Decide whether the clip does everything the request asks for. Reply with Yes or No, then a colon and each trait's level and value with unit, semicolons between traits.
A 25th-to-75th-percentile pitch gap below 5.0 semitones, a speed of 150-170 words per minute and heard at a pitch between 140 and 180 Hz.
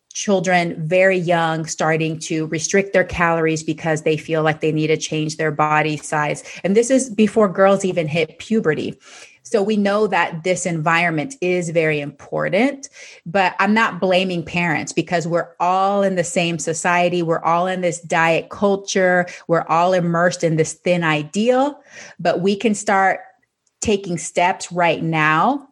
Yes: average, 3.2 semitones; average, 160 wpm; medium, 175 Hz